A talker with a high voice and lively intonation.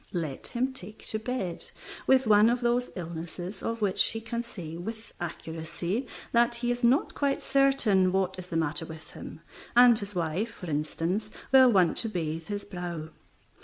Yes: high, 200 Hz; wide, 5.7 semitones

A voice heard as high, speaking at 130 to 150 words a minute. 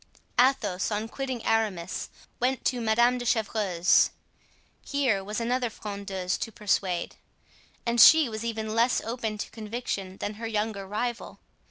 Yes: high, 220 Hz; average, 140 wpm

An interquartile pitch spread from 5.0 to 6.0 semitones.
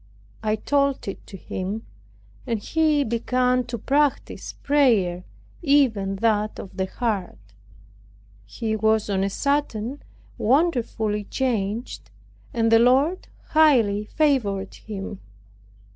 Yes: average, 5.3 semitones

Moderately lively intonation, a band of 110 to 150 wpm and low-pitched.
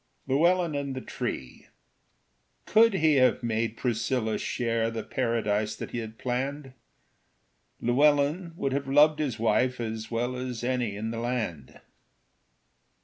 Yes: average, 3.8 semitones; slow, 135 wpm; low, 125 Hz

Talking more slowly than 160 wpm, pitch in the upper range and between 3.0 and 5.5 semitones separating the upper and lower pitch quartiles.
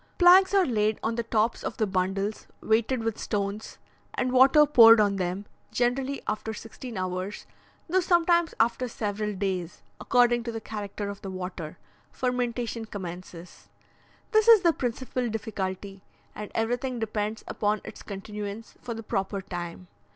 Yes: average, 150 wpm; high, 220 Hz; average, 3.8 semitones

